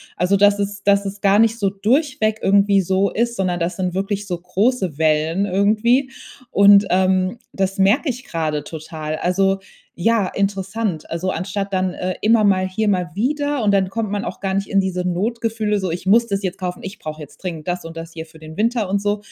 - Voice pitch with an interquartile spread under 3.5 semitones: Yes, narrow, 2.6 semitones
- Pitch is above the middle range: Yes, high, 195 Hz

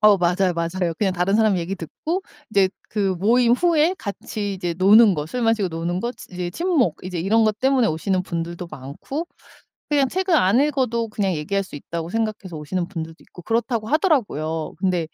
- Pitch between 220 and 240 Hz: No, high, 195 Hz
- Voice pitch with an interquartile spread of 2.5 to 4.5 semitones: No, average, 5.2 semitones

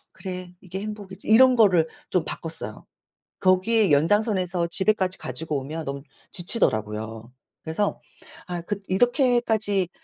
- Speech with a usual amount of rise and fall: Yes, average, 4.8 semitones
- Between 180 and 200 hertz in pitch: Yes, medium, 185 Hz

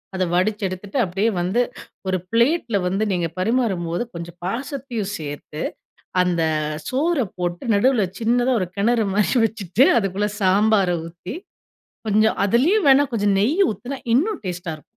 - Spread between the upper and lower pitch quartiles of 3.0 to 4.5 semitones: No, average, 5.0 semitones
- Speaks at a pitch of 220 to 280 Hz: No, high, 205 Hz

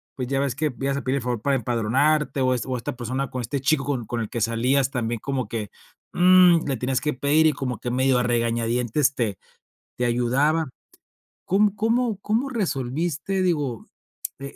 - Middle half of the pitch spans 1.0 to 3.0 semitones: No, average, 4.0 semitones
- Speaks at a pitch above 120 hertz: Yes, low, 135 Hz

